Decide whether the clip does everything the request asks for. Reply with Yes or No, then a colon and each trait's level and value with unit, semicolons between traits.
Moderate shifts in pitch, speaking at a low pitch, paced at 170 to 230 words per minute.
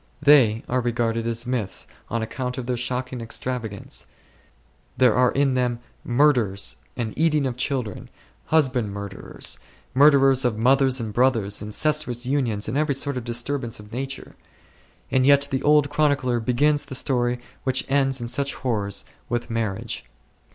No: average, 3.0 semitones; low, 125 Hz; average, 150 wpm